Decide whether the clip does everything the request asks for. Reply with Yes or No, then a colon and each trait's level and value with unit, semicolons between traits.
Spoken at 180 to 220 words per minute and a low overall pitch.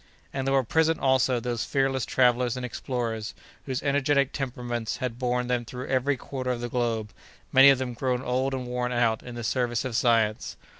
Yes: average, 195 wpm; low, 125 Hz